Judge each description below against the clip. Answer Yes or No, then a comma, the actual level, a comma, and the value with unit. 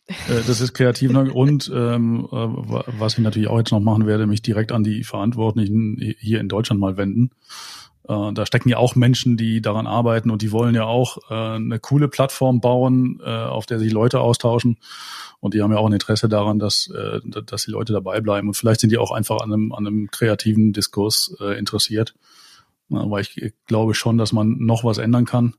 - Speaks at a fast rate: Yes, fast, 205 wpm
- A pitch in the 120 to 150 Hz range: No, low, 110 Hz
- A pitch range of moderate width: No, narrow, 1.9 semitones